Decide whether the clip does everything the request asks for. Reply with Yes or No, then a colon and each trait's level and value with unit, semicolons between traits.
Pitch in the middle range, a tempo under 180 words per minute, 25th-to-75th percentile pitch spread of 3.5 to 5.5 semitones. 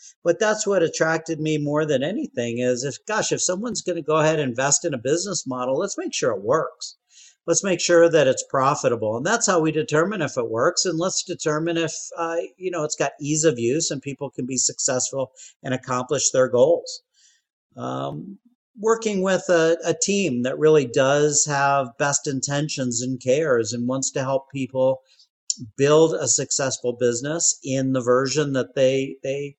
No: medium, 155 Hz; average, 185 wpm; average, 5.1 semitones